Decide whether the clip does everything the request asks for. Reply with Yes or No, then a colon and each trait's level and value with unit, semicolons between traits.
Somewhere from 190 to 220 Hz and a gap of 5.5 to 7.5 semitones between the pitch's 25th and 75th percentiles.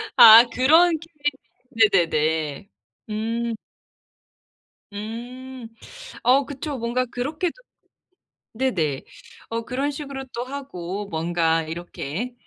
No: high, 235 Hz; wide, 5.9 semitones